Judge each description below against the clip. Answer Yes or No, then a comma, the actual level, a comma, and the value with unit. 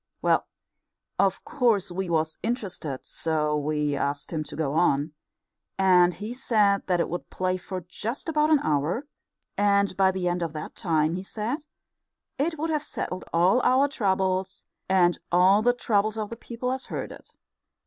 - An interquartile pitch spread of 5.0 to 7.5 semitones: Yes, wide, 5.5 semitones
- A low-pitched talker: No, high, 190 Hz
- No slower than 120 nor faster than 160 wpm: No, average, 170 wpm